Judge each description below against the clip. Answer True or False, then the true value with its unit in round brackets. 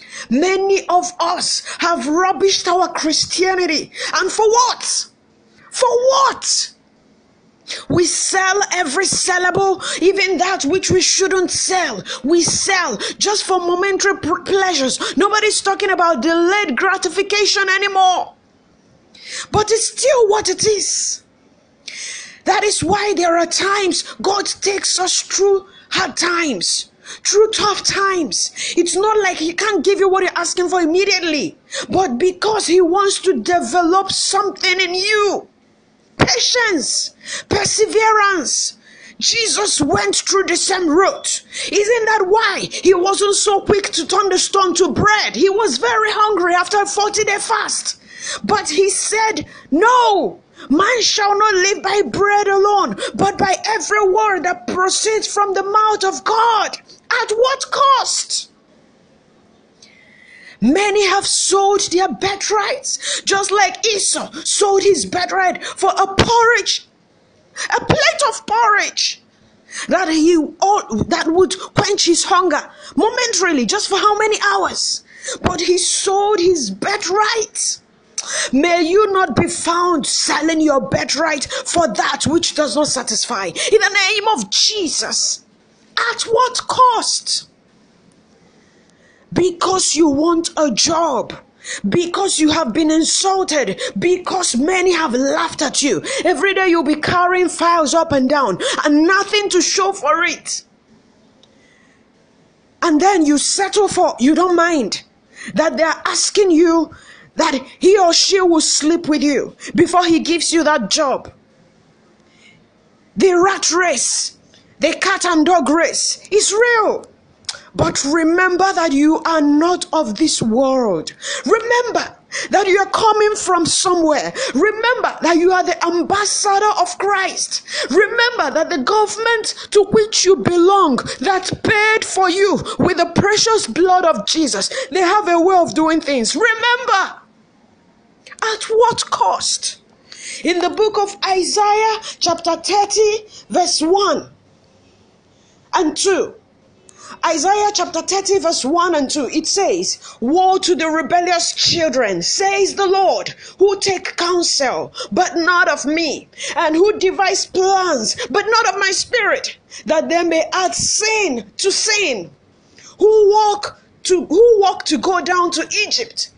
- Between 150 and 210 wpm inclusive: False (135 wpm)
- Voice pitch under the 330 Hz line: False (370 Hz)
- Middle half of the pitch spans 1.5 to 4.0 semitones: True (3.5 semitones)